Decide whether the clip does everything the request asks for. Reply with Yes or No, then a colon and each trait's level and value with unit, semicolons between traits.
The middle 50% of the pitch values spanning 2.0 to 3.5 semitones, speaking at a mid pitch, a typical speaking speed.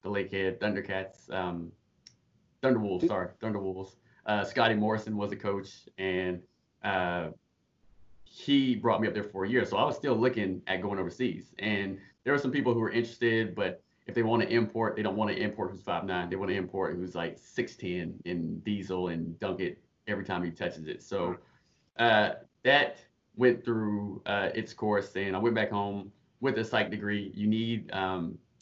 No: average, 3.1 semitones; low, 100 Hz; average, 190 wpm